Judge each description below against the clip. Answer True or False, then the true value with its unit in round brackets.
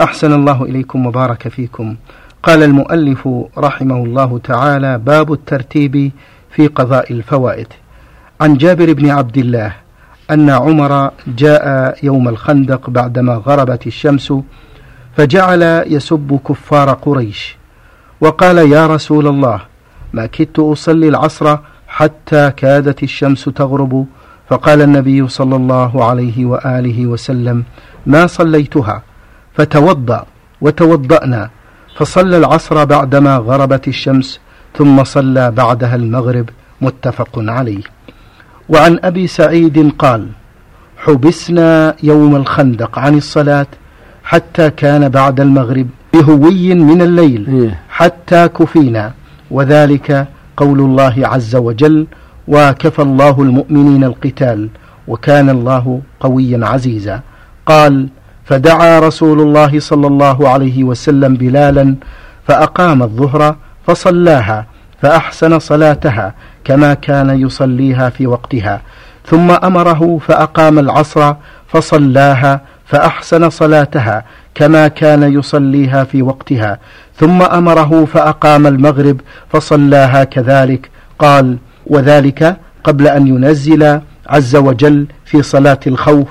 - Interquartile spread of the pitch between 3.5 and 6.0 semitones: False (3.0 semitones)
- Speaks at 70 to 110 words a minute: True (100 wpm)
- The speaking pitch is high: False (140 Hz)